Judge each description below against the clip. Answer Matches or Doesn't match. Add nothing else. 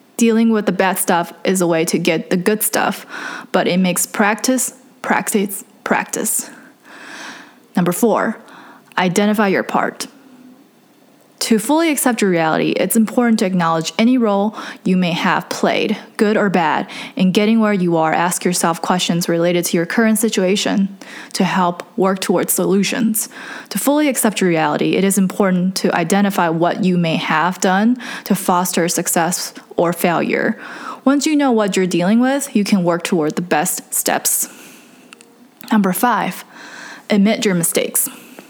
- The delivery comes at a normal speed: Matches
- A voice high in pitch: Matches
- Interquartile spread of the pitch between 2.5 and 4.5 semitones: Doesn't match